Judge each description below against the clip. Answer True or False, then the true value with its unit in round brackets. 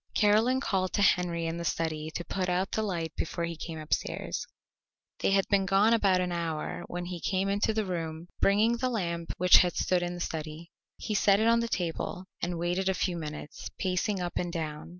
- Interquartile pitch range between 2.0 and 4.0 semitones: True (2.8 semitones)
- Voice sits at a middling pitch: True (180 Hz)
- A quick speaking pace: True (210 wpm)